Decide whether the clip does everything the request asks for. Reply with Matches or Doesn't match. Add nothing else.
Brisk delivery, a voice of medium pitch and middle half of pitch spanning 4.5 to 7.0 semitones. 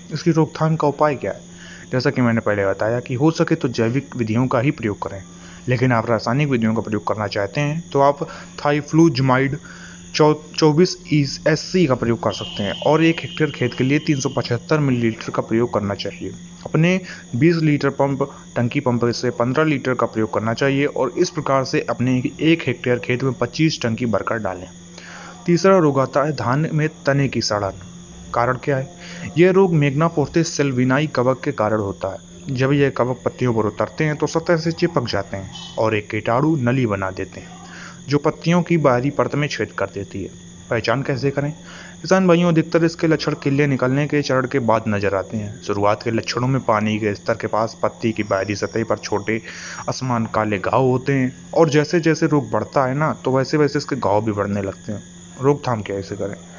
Doesn't match